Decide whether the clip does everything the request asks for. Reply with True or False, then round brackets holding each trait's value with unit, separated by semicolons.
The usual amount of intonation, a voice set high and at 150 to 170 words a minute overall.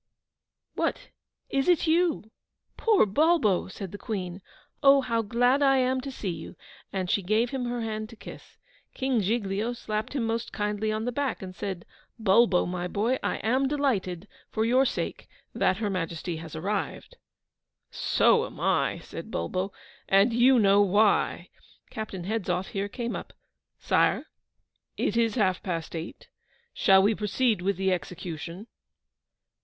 True (4.5 semitones; 215 Hz; 155 wpm)